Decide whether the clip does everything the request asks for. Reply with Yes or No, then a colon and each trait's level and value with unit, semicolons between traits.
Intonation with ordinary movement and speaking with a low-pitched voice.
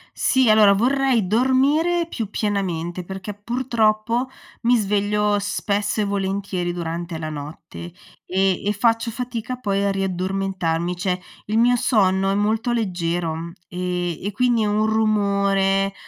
No: average, 3.4 semitones; high, 200 Hz